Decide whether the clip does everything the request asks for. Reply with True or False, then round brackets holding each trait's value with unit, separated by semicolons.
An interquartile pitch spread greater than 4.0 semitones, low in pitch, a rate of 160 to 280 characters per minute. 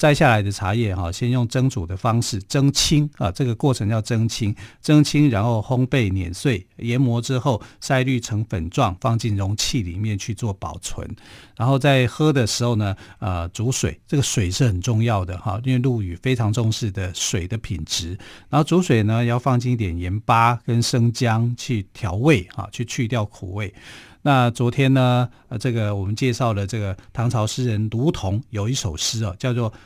False (3.6 semitones; 115 Hz; 270 characters per minute)